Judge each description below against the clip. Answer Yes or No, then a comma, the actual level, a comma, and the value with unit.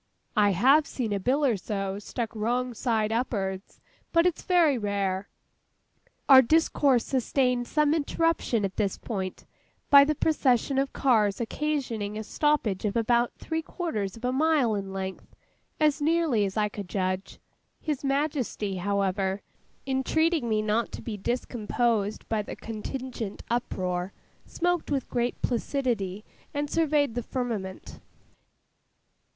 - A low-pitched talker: No, high, 235 Hz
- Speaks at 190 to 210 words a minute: No, slow, 135 wpm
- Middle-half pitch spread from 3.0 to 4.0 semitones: No, wide, 5.5 semitones